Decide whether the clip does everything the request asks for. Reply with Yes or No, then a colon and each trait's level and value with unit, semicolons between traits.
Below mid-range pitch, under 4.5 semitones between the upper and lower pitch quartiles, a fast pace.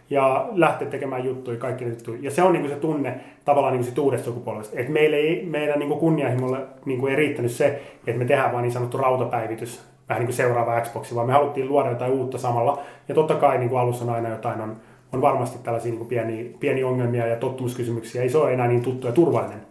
Yes: low, 125 Hz; average, 2.9 semitones; fast, 205 wpm